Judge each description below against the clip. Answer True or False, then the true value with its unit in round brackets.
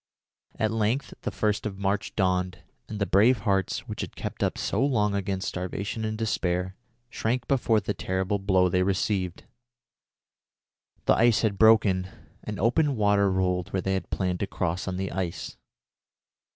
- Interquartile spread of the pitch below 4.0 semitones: True (2.7 semitones)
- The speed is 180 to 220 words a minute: False (165 wpm)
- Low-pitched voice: True (100 Hz)